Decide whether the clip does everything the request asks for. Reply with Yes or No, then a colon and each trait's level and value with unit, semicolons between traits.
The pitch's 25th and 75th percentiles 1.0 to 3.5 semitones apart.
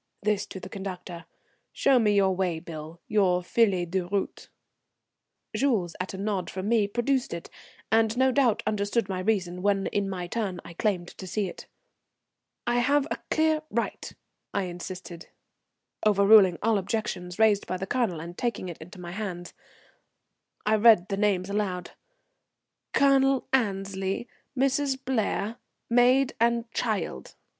No: average, 4.1 semitones